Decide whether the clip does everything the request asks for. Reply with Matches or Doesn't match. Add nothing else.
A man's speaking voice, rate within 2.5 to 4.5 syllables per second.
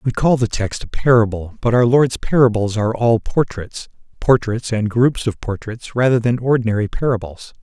Doesn't match